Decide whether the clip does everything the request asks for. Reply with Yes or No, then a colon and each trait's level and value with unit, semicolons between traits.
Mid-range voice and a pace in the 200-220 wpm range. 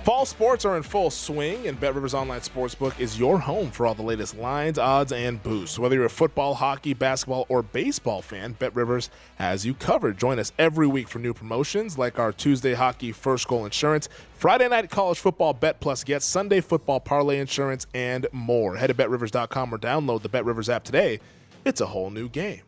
No: low, 130 Hz; fast, 205 wpm